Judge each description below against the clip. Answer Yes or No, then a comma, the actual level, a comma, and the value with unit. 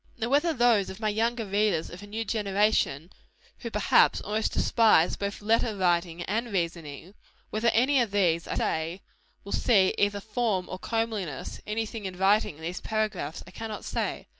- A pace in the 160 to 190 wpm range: Yes, average, 170 wpm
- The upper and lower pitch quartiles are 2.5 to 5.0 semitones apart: Yes, average, 3.6 semitones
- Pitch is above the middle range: Yes, high, 205 Hz